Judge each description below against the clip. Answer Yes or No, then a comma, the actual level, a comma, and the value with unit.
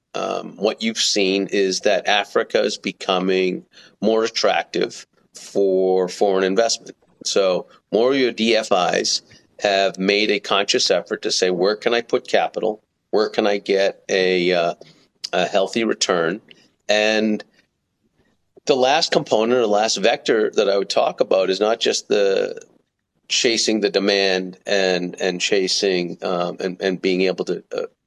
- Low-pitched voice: Yes, low, 100 Hz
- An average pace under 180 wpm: Yes, average, 150 wpm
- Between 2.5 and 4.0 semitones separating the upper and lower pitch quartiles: Yes, average, 3.1 semitones